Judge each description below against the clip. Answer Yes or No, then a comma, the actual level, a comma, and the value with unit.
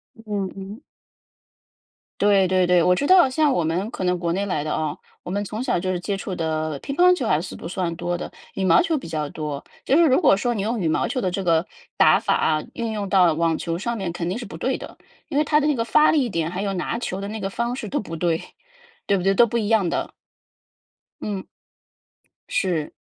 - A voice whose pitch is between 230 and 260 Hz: No, high, 195 Hz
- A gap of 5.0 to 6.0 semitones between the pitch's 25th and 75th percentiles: Yes, average, 5.3 semitones